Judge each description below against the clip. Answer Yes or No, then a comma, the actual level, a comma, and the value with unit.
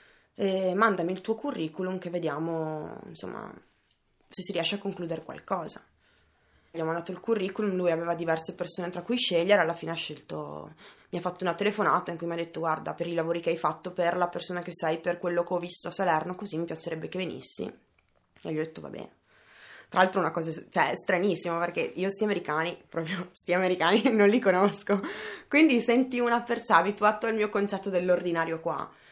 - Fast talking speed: Yes, fast, 200 wpm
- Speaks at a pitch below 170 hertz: No, medium, 175 Hz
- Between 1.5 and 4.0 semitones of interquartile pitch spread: Yes, average, 3.1 semitones